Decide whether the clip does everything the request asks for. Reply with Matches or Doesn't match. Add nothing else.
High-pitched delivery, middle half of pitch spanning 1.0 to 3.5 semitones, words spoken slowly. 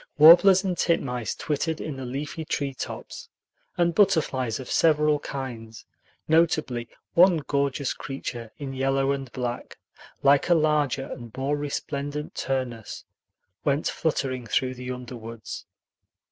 Doesn't match